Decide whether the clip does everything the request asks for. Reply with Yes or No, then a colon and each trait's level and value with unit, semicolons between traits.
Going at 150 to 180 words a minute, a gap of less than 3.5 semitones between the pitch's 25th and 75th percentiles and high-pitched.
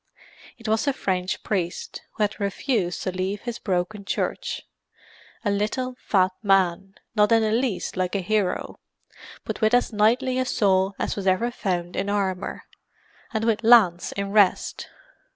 Yes: average, 160 wpm; average, 3.0 semitones; high, 200 Hz